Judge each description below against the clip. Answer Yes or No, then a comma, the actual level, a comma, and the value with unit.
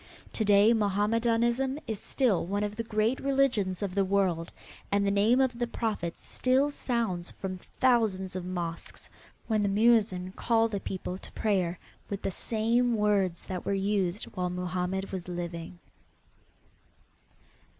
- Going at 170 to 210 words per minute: No, average, 150 wpm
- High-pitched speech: Yes, high, 200 Hz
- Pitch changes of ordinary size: Yes, average, 3.7 semitones